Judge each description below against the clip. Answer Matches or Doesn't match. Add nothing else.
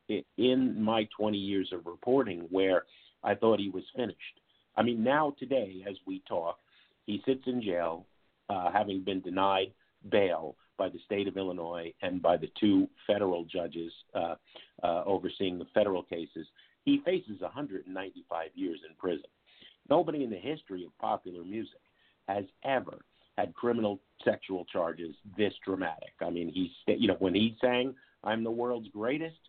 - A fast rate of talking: Doesn't match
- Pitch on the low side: Matches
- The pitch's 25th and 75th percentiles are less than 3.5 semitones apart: Doesn't match